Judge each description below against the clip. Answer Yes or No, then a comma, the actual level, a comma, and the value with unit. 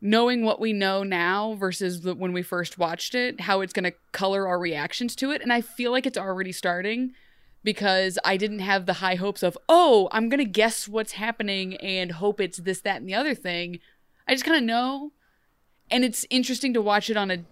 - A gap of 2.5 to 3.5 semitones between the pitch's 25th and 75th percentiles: No, average, 4.4 semitones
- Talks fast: Yes, fast, 225 wpm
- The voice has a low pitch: No, high, 205 Hz